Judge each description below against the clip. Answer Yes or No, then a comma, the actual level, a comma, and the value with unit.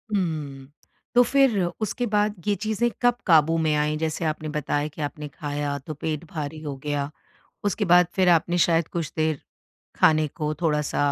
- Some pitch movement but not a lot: Yes, average, 3.1 semitones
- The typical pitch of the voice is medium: Yes, medium, 155 Hz